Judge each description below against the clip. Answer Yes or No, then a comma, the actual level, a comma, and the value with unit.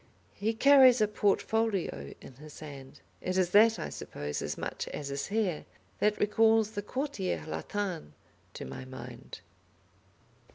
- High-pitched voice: Yes, high, 205 Hz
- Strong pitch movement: Yes, wide, 7.1 semitones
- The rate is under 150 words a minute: Yes, average, 140 wpm